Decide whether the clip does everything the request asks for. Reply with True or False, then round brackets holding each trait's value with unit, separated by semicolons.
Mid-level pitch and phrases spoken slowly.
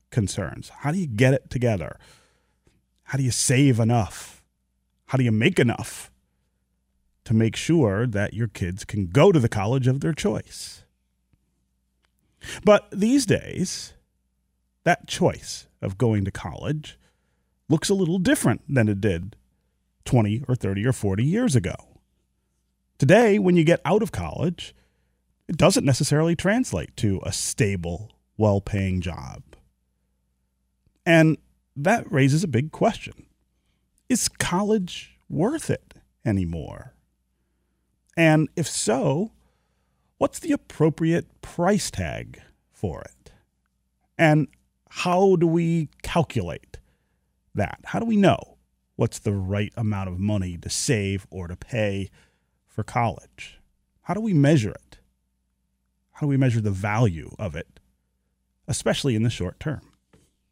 False (105 Hz; 130 wpm)